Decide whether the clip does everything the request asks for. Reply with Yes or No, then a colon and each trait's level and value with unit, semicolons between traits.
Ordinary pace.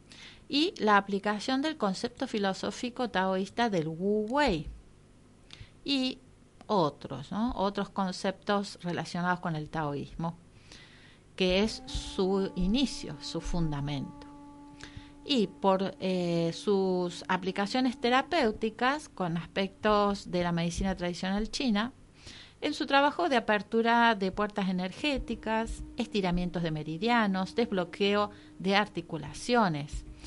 No: slow, 105 wpm